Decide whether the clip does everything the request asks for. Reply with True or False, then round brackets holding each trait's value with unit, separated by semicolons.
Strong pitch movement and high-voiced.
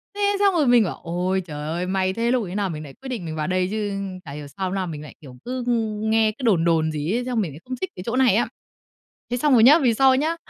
True (6.8 semitones; 205 Hz)